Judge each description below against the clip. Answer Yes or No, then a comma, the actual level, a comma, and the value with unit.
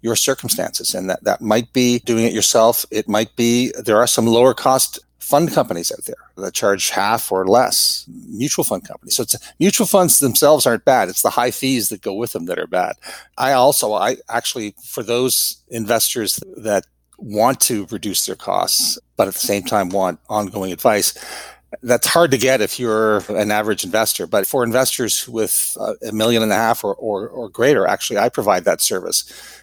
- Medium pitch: No, low, 115 Hz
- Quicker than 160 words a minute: Yes, average, 195 wpm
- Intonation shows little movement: No, average, 3.1 semitones